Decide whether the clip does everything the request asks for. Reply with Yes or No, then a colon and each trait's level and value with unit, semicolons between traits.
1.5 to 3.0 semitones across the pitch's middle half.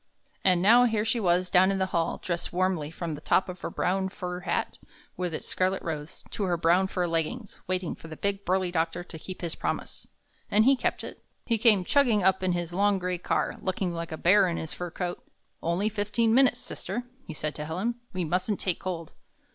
Yes: average, 2.7 semitones